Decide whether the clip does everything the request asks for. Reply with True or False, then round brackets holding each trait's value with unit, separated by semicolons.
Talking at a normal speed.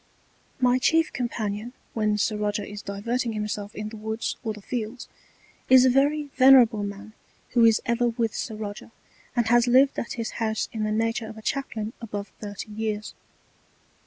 True (175 wpm)